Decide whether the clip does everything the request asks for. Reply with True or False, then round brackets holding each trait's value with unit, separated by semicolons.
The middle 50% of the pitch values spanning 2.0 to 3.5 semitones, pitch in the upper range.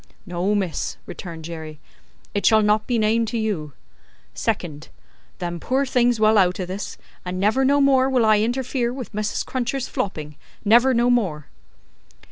False (5.3 semitones; 215 Hz)